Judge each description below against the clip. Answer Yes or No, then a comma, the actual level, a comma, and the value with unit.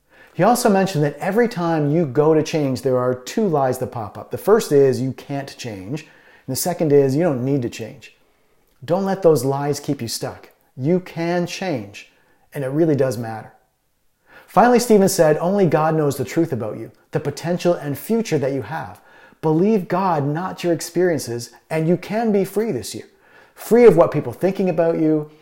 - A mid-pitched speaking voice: Yes, medium, 155 Hz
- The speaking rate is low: No, average, 195 wpm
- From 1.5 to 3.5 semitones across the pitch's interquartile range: No, average, 4.9 semitones